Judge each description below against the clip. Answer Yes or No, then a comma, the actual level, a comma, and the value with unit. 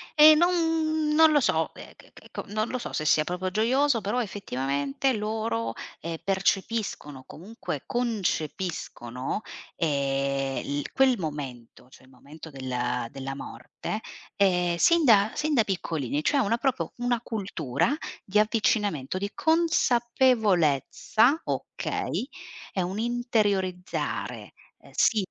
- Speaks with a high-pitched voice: Yes, high, 200 Hz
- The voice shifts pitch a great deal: Yes, wide, 8.6 semitones